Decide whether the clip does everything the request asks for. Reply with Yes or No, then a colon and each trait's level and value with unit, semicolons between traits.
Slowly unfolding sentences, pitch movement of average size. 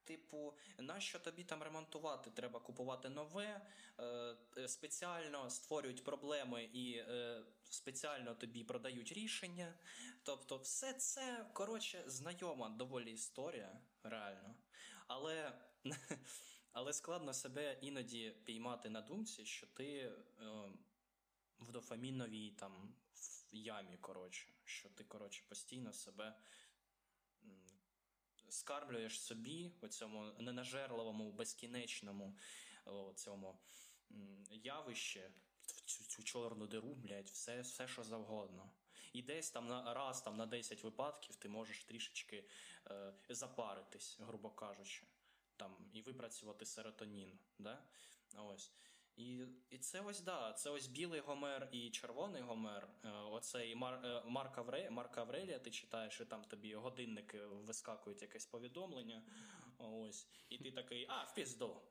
No: average, 115 wpm; average, 4.9 semitones